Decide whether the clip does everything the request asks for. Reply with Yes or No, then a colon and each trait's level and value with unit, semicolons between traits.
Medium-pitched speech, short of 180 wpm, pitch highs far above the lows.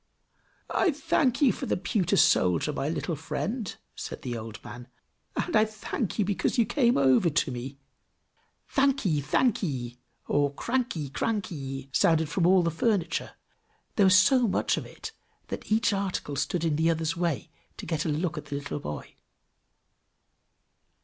Yes: medium, 165 Hz; average, 160 wpm; wide, 6.8 semitones